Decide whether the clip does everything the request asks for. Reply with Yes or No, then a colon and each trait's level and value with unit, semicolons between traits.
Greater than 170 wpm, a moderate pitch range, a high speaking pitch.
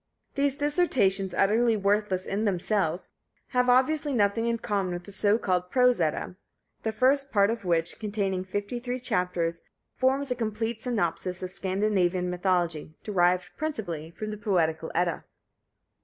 No: average, 145 wpm; average, 4.7 semitones; high, 200 Hz